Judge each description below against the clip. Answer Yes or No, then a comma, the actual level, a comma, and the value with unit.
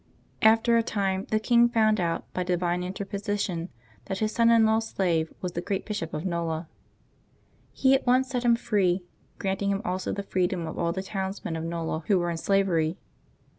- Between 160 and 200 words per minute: Yes, average, 195 wpm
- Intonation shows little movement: No, average, 3.9 semitones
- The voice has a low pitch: No, high, 195 Hz